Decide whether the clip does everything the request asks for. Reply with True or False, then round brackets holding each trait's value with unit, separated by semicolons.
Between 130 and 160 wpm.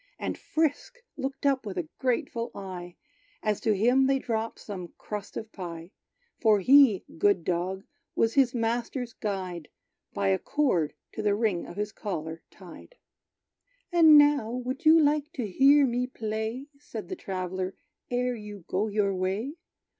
True (155 wpm)